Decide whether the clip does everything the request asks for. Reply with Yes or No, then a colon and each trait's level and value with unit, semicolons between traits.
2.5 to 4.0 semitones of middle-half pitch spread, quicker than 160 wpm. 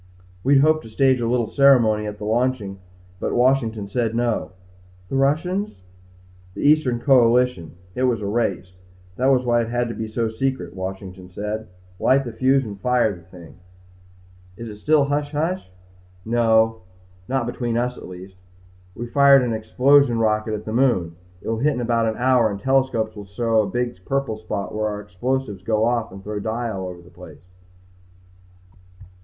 Yes: average, 3.7 semitones; average, 180 wpm